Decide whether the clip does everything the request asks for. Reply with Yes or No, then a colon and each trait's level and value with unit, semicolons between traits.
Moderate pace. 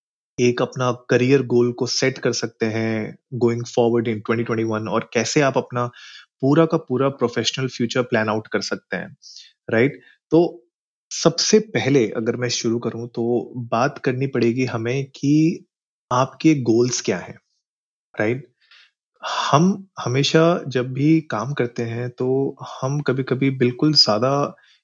Yes: average, 145 wpm